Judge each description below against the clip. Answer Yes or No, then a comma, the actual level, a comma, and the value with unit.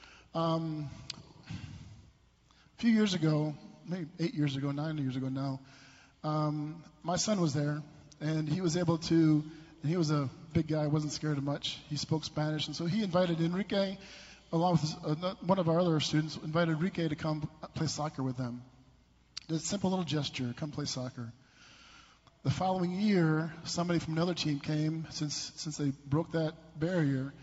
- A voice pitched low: No, medium, 155 Hz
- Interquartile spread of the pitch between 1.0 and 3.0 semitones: Yes, narrow, 2.4 semitones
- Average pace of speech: Yes, average, 175 wpm